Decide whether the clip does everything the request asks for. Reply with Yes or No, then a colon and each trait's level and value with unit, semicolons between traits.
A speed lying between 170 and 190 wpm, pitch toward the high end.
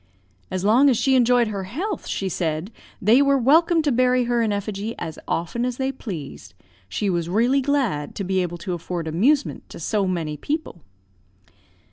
Yes: average, 180 wpm; high, 215 Hz